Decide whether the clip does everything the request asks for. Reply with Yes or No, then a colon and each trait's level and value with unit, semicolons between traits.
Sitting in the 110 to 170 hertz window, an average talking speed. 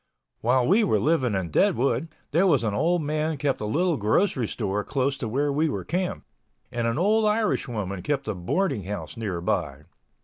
Yes: low, 135 Hz; average, 190 wpm